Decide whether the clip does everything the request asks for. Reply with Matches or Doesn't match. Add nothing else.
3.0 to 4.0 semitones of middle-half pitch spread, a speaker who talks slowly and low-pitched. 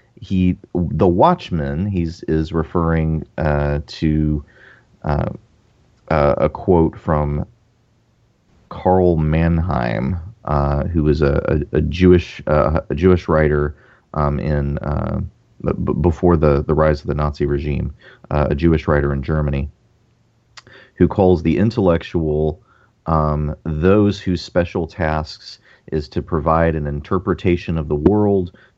Matches